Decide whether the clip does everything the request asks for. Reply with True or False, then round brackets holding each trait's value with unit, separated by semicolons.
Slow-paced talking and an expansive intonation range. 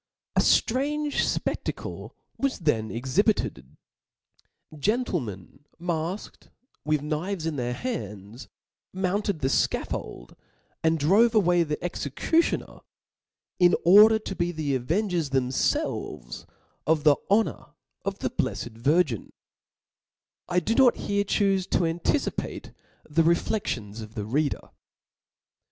True (115 wpm; 7.3 semitones)